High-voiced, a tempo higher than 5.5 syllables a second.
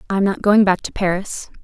Yes: high, 195 Hz; 6.0 syllables/s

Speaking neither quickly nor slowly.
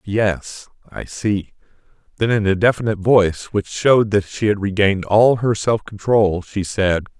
Yes: average, 165 wpm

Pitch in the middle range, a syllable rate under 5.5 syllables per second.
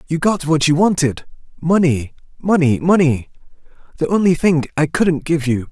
Yes: medium, 155 Hz; 4.7 syllables/s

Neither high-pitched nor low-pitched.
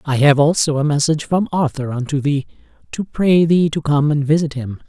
Yes: medium, 150 Hz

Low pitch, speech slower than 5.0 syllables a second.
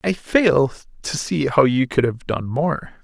No: medium, 145 Hz; 3.9 syllables/s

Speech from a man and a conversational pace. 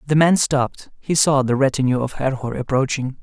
Yes: male; average, 185 wpm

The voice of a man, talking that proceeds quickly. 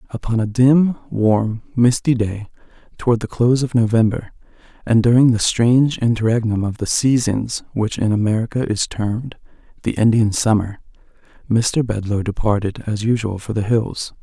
No: male; average, 150 wpm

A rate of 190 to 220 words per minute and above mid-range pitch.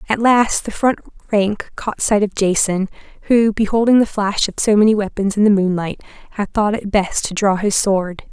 Yes: average, 200 wpm; high, 205 Hz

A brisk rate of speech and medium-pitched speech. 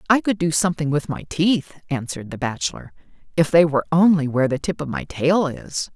Yes: fast, 210 wpm; medium, 150 Hz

